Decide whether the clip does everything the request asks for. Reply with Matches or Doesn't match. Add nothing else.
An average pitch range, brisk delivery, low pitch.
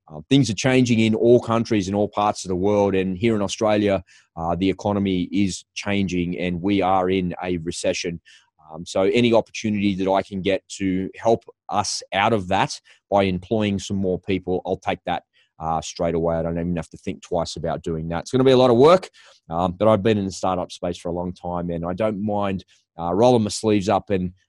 Matches